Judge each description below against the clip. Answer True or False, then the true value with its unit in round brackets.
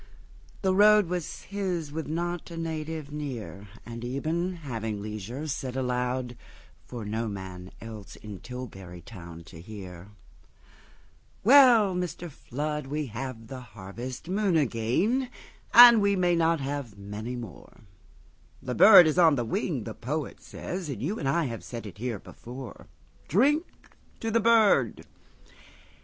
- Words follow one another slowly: True (125 wpm)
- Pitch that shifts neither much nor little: False (7.7 semitones)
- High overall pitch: False (135 Hz)